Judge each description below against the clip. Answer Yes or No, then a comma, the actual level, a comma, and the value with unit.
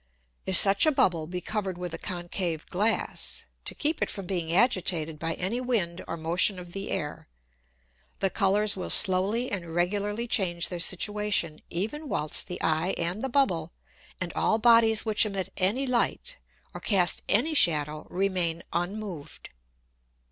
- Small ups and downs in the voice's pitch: No, average, 3.8 semitones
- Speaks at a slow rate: No, average, 155 wpm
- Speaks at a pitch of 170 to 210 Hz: Yes, high, 190 Hz